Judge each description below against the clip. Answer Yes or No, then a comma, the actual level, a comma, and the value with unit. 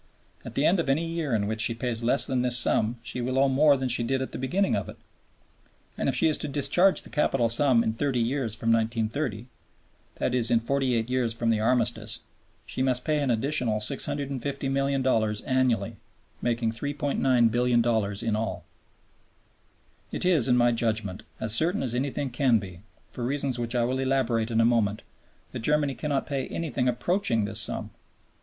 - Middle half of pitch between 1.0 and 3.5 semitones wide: Yes, average, 3.2 semitones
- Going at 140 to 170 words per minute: No, average, 185 wpm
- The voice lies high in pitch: No, low, 125 Hz